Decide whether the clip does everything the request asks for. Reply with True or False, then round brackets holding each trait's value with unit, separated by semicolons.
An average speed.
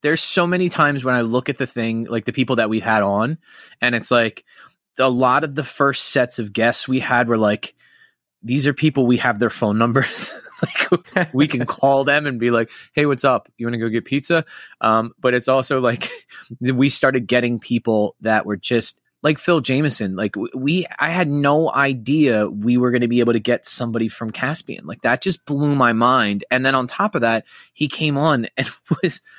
False (215 wpm)